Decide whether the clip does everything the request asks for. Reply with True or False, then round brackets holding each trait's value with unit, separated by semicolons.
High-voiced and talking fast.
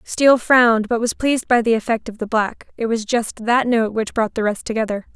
True (230 Hz; 235 wpm)